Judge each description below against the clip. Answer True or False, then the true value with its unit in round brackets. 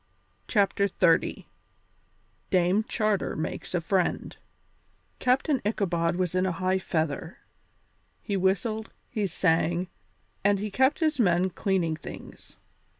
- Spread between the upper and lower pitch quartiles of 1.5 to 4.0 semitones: True (3.4 semitones)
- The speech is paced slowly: True (110 wpm)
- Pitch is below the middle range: False (190 Hz)